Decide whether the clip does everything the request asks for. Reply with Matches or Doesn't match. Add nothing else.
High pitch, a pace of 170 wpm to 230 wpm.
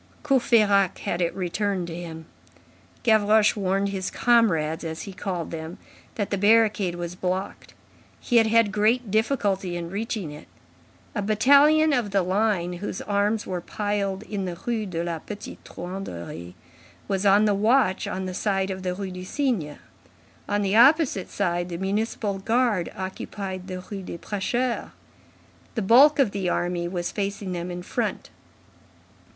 Doesn't match